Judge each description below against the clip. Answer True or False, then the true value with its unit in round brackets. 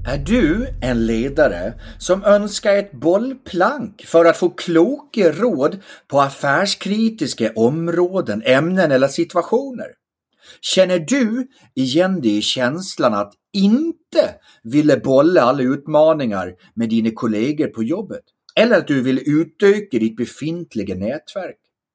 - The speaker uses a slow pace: True (120 wpm)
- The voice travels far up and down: True (8.1 semitones)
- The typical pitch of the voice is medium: True (170 Hz)